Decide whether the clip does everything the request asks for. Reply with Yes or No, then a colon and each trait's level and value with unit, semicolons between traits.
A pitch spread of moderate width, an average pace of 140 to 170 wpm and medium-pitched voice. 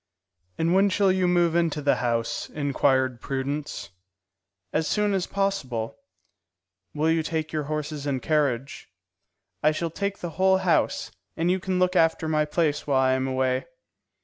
Yes: average, 4.5 semitones; average, 160 wpm; medium, 155 Hz